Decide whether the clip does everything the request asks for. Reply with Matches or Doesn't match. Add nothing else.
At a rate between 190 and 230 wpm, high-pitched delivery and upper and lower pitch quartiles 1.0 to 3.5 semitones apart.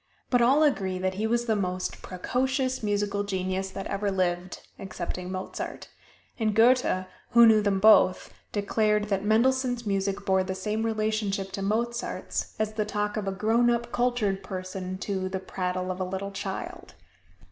Doesn't match